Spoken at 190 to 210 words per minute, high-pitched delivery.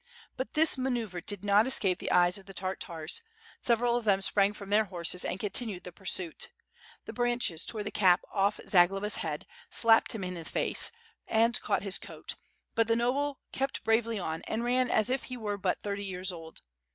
Yes: average, 195 wpm; high, 205 Hz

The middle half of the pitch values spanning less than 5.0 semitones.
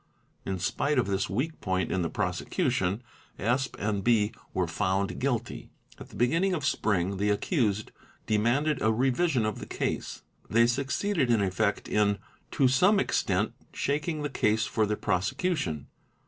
No: wide, 5.6 semitones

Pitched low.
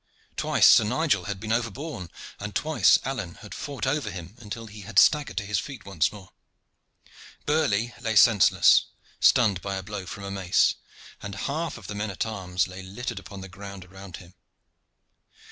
Yes: low, 105 Hz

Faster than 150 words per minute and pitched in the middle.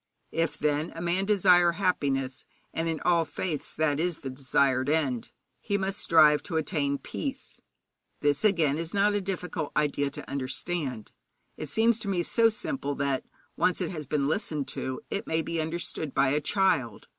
Yes: average, 180 wpm; medium, 160 Hz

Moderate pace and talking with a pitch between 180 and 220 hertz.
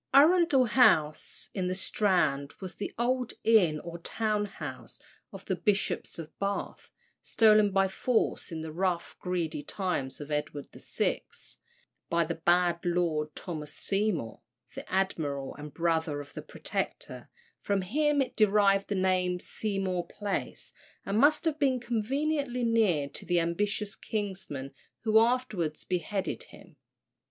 Yes: average, 145 wpm; high, 190 Hz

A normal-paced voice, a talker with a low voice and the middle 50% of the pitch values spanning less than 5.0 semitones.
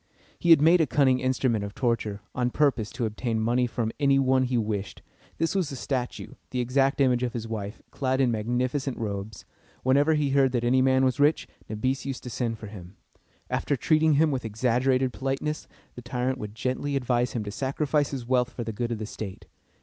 No: fast, 210 wpm; low, 125 Hz; average, 3.0 semitones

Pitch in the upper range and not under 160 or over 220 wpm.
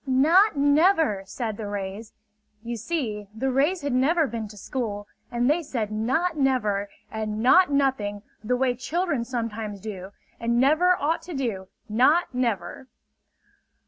No: high, 245 Hz; average, 145 wpm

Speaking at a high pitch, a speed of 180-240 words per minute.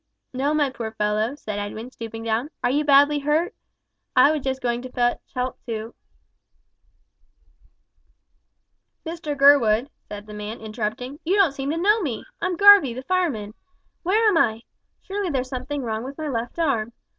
No: very high, 260 Hz; average, 170 wpm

